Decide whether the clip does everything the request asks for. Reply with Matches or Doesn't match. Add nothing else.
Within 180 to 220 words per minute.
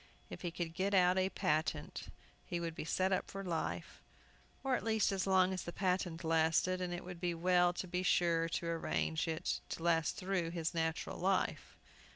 Matches